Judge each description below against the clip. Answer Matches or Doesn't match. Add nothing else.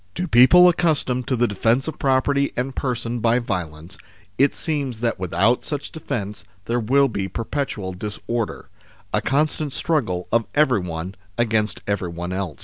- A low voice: Matches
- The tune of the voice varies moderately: Doesn't match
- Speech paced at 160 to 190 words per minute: Doesn't match